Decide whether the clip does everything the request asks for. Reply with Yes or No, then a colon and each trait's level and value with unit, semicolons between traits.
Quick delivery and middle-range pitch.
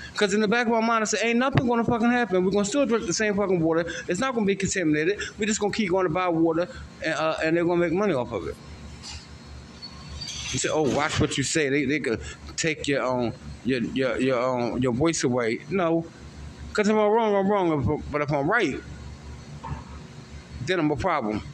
Yes: fast, 225 wpm; medium, 160 Hz